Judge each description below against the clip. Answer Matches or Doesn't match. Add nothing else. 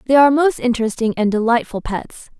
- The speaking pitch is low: Doesn't match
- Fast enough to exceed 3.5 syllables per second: Matches